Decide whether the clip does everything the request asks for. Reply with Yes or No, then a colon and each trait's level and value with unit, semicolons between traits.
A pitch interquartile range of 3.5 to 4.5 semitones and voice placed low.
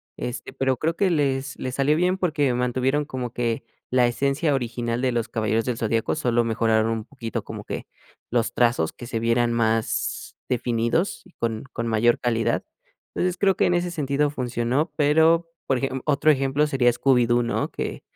Yes: average, 3.8 semitones; low, 125 Hz